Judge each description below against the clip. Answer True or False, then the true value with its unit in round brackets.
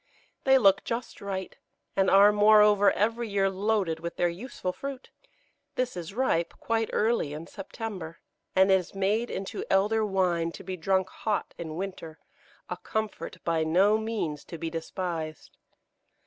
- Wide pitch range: False (4.1 semitones)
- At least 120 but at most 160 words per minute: True (150 wpm)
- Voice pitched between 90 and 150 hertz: False (195 Hz)